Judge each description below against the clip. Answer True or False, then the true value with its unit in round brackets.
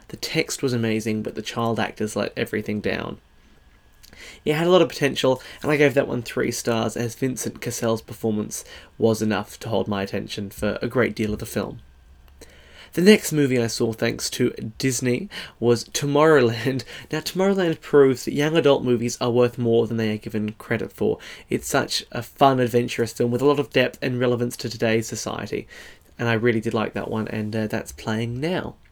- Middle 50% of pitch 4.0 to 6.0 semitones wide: False (3.2 semitones)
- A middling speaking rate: True (195 wpm)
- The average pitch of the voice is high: False (115 Hz)